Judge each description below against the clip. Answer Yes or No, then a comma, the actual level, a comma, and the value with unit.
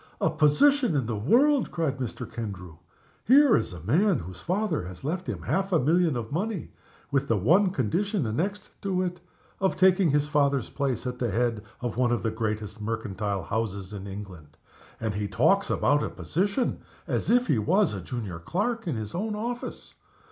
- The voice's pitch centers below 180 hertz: Yes, medium, 140 Hz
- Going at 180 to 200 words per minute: Yes, average, 185 wpm